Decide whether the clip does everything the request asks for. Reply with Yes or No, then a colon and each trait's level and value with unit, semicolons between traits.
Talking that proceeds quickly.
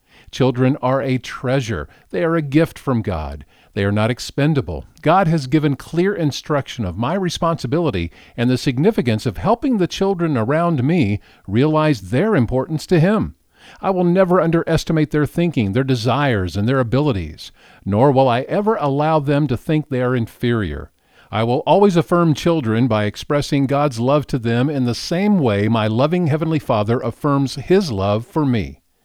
No: average, 170 wpm